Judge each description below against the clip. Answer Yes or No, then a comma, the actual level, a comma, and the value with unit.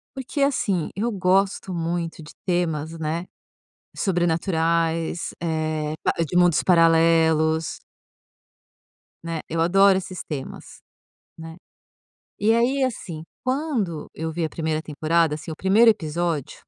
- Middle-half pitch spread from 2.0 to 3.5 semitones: Yes, average, 3.0 semitones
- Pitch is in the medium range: Yes, medium, 170 Hz